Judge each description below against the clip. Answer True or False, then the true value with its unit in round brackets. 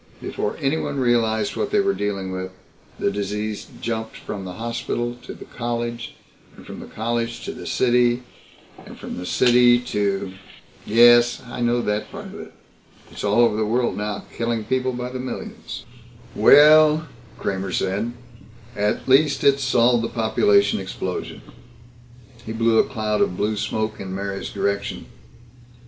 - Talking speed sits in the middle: True (160 wpm)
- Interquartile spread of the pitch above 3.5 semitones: False (2.9 semitones)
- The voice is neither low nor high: False (115 Hz)